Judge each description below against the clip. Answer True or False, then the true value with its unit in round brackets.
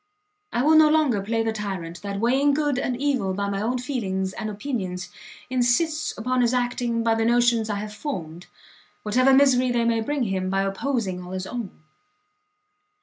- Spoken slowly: False (180 wpm)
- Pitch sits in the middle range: False (230 Hz)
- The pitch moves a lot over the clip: False (4.3 semitones)